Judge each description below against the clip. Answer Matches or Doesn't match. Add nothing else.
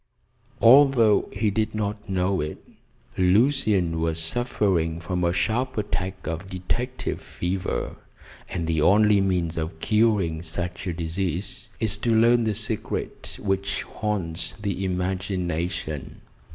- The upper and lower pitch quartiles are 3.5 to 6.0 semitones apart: Matches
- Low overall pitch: Matches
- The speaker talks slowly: Matches